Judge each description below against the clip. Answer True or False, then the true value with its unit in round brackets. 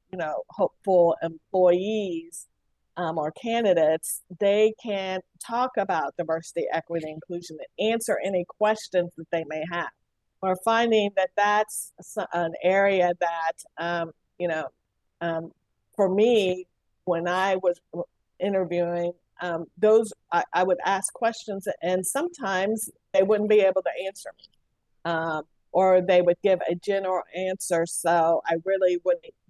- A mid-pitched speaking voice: True (180 Hz)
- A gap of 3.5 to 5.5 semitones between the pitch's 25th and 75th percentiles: False (3.0 semitones)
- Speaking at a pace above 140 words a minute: False (135 wpm)